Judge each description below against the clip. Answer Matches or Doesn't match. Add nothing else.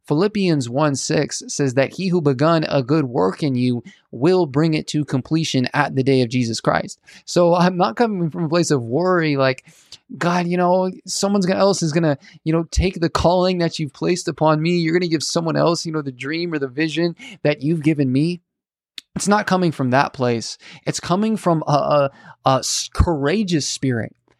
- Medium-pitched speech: Matches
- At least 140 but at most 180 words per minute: Doesn't match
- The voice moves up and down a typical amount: Matches